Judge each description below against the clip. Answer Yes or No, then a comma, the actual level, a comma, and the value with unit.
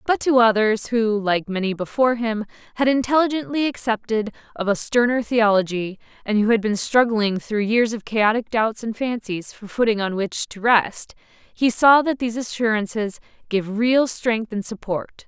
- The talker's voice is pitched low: No, high, 225 Hz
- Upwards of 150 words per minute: Yes, average, 170 wpm